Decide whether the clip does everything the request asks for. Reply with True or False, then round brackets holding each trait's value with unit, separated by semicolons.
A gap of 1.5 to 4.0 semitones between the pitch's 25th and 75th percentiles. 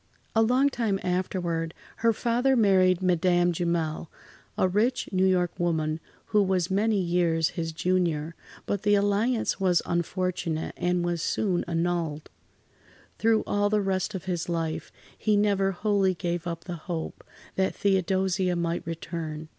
True (3.0 semitones)